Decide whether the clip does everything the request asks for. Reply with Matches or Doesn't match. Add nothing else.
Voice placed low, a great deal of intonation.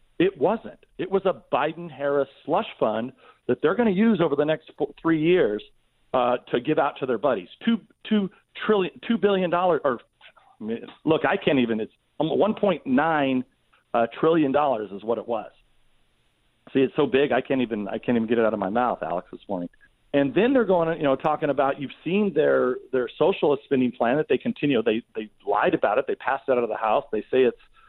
Doesn't match